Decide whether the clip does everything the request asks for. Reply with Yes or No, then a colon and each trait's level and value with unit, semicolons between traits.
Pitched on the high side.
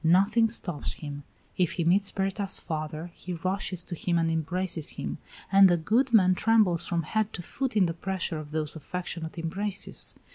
No: medium, 180 Hz